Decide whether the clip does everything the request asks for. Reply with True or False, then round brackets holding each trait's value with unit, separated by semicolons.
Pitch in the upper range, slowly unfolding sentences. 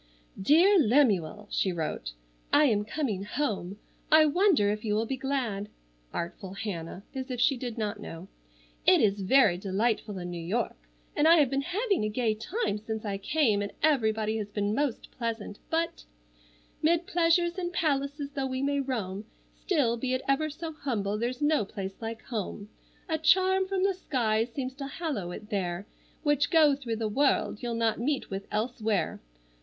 False (235 Hz; 175 wpm)